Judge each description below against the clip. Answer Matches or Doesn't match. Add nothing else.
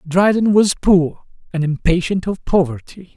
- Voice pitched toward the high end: Doesn't match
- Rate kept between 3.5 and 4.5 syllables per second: Matches